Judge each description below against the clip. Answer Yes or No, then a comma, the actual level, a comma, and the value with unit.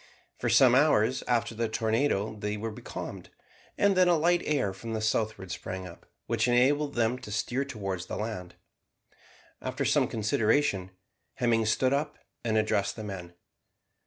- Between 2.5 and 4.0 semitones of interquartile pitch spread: Yes, average, 3.7 semitones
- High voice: No, low, 115 Hz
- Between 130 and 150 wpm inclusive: No, average, 160 wpm